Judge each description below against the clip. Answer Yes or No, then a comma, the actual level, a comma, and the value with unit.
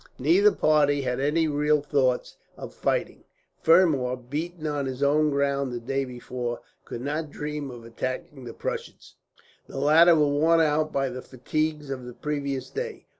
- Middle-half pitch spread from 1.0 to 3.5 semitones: Yes, average, 3.1 semitones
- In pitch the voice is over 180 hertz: No, medium, 145 Hz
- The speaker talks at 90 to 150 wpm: No, average, 165 wpm